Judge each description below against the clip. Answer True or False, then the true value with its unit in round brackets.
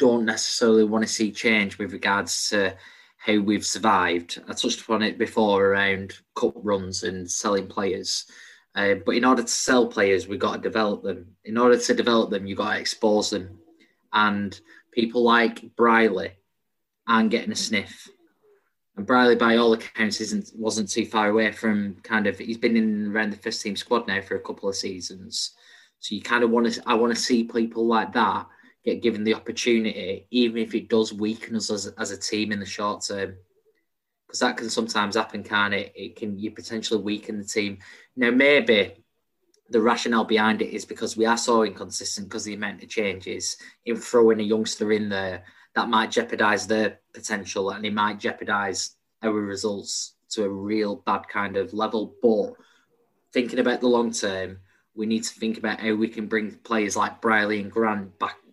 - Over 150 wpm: True (190 wpm)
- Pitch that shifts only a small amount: True (2.2 semitones)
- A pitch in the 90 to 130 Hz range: True (110 Hz)